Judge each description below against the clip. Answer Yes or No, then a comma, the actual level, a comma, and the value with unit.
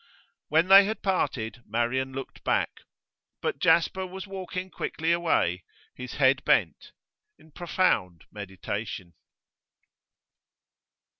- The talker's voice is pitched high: No, medium, 150 Hz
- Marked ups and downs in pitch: Yes, wide, 8.7 semitones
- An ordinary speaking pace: No, slow, 100 wpm